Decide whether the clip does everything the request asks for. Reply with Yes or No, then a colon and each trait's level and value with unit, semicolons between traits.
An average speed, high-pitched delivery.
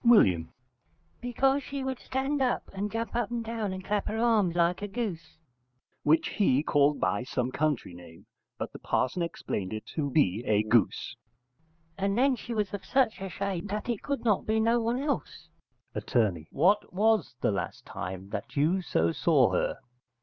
Yes: average, 180 wpm; high, 195 Hz